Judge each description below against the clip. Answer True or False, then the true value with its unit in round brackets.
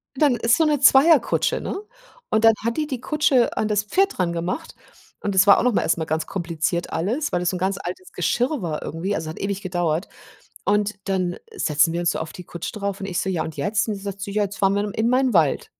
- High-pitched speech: True (200 Hz)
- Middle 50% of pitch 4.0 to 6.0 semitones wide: True (4.9 semitones)